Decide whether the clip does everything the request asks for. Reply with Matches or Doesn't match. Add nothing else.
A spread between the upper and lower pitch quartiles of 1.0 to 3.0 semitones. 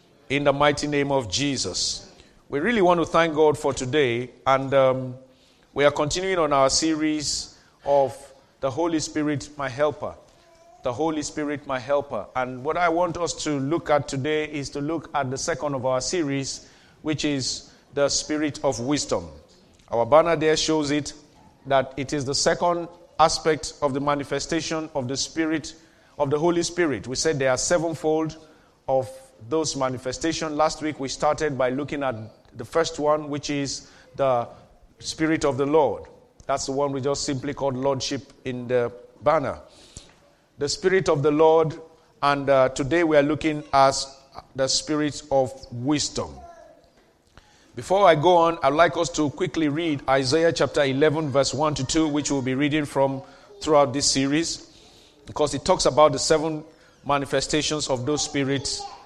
Matches